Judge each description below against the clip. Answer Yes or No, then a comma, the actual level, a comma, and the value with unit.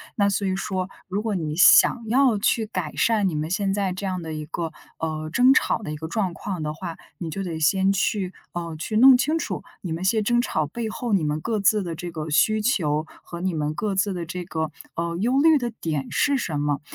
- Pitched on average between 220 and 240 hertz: No, medium, 185 Hz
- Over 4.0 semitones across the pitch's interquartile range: Yes, average, 5.0 semitones